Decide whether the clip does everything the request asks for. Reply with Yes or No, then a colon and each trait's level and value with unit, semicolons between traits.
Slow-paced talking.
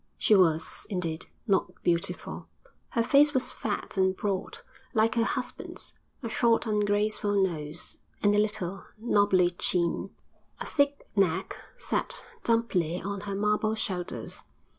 Yes: slow, 130 wpm